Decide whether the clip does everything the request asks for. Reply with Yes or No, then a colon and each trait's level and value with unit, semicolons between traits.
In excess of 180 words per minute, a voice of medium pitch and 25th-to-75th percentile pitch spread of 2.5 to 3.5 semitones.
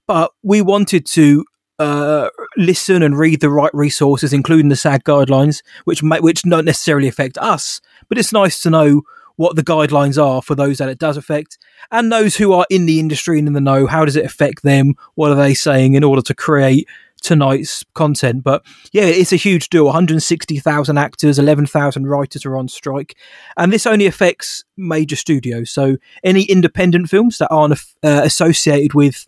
Yes: average, 195 wpm; medium, 150 Hz; average, 3.2 semitones